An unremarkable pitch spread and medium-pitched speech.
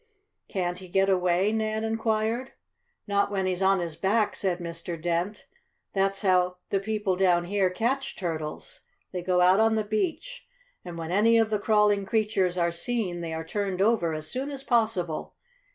No: average, 3.6 semitones; high, 195 Hz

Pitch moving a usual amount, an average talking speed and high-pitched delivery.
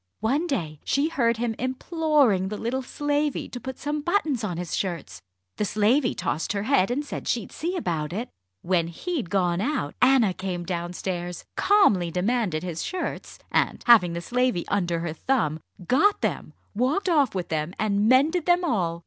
No: wide, 8.0 semitones; average, 175 wpm; high, 225 Hz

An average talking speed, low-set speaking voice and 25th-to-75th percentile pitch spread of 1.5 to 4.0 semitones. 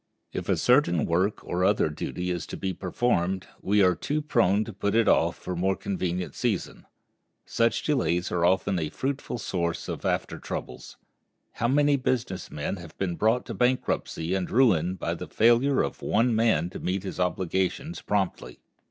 No: average, 180 wpm; very low, 95 Hz; average, 4.8 semitones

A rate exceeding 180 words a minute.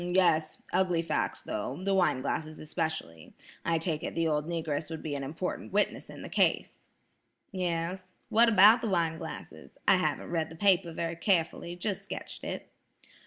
No: average, 175 wpm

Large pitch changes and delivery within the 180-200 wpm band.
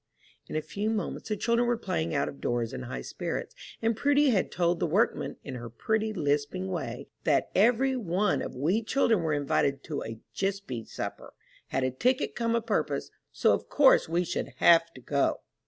Yes: wide, 8.1 semitones; average, 195 wpm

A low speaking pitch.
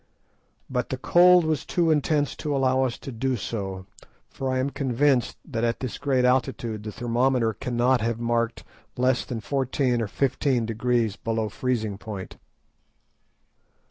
Yes: low, 125 Hz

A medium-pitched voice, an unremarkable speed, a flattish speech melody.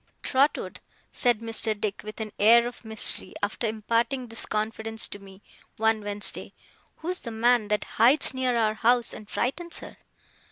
No: high, 225 Hz; average, 160 wpm; narrow, 2.1 semitones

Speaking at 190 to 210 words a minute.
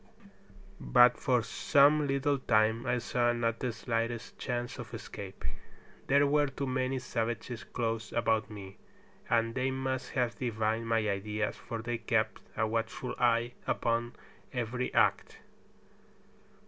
No: slow, 135 wpm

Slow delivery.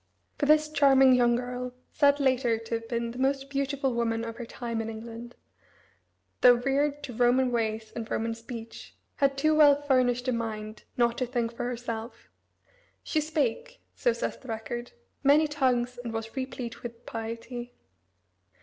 No: average, 165 wpm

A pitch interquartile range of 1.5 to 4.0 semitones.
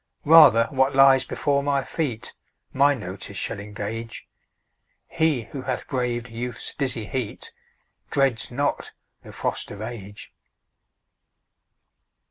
Yes: average, 3.5 semitones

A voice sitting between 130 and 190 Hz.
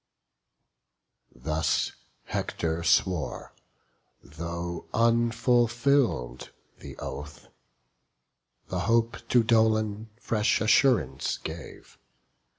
No: low, 105 Hz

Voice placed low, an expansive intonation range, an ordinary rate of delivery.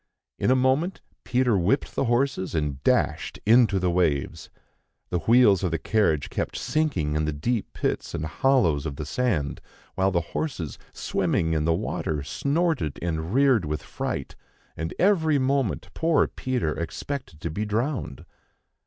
Yes: low, 100 Hz; wide, 8.8 semitones; average, 155 wpm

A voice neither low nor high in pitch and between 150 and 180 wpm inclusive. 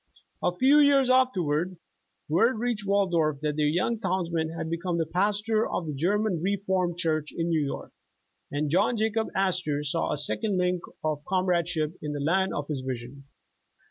Yes: medium, 175 Hz; average, 170 wpm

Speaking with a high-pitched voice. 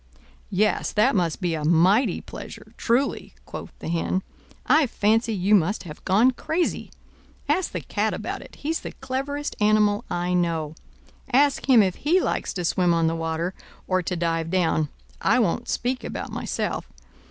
Yes: high, 195 Hz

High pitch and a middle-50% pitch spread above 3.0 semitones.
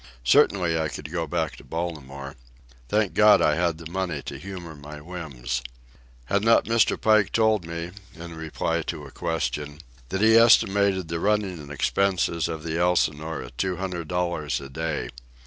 No: very low, 85 Hz; average, 3.7 semitones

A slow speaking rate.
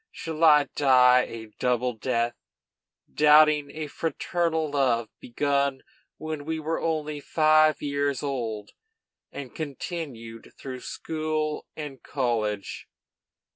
Yes: slow, 105 wpm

